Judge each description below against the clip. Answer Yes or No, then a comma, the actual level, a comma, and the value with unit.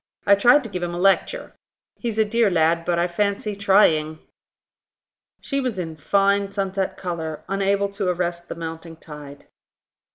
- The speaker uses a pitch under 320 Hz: Yes, high, 190 Hz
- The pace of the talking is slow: No, average, 160 wpm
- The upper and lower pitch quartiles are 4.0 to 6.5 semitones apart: No, average, 3.3 semitones